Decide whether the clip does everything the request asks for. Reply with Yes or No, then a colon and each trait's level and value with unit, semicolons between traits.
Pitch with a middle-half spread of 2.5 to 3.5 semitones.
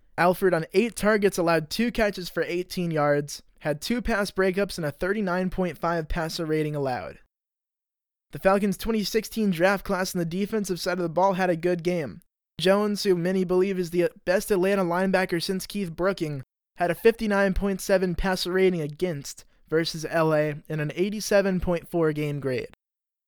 Yes: average, 2.8 semitones